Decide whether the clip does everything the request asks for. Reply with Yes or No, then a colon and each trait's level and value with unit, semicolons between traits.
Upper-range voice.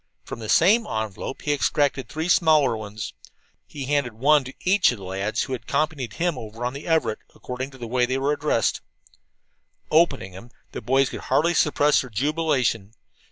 No: low, 135 Hz